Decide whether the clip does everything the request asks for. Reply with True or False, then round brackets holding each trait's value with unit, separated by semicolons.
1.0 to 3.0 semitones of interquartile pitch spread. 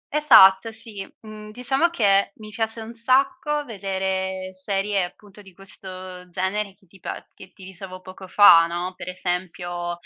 True (2.6 semitones)